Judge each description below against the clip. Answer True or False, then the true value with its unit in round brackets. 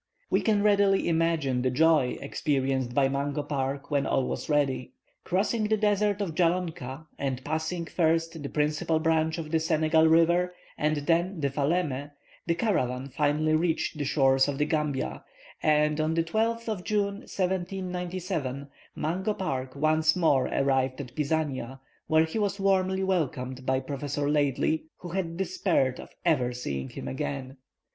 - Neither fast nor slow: True (155 wpm)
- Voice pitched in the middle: True (155 Hz)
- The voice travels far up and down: False (4.5 semitones)